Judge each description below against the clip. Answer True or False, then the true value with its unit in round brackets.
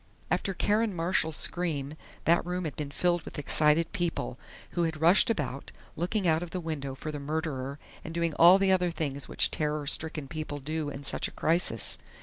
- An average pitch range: True (3.0 semitones)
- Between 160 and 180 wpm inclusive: False (190 wpm)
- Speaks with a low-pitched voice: False (160 Hz)